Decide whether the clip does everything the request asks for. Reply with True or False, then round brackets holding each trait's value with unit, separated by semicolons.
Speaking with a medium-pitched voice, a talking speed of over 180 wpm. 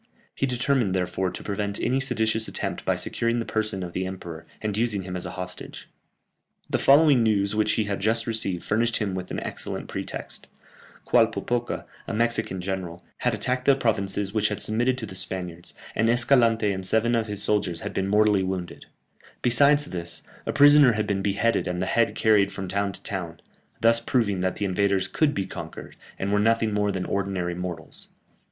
False (105 Hz; 190 wpm)